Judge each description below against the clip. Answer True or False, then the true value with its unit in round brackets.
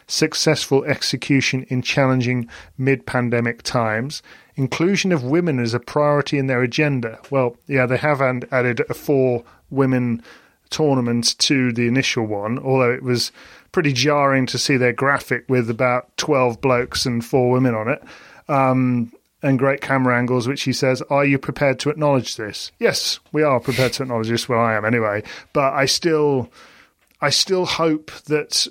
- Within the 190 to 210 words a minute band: False (165 wpm)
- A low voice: True (130 Hz)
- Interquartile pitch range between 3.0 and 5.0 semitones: False (2.5 semitones)